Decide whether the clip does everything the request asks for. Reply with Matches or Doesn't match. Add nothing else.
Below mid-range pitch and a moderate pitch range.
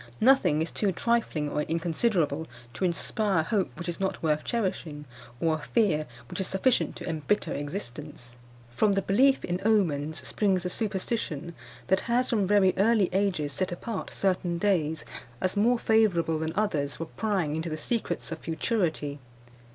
Doesn't match